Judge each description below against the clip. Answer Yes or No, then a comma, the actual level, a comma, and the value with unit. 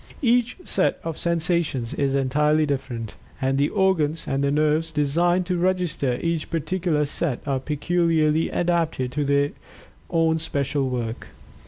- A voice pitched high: No, medium, 155 Hz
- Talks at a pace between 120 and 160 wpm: Yes, slow, 135 wpm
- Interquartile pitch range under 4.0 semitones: Yes, average, 3.4 semitones